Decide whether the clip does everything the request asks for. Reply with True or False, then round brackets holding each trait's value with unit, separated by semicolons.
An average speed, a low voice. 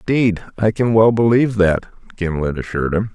True (170 wpm; 100 Hz)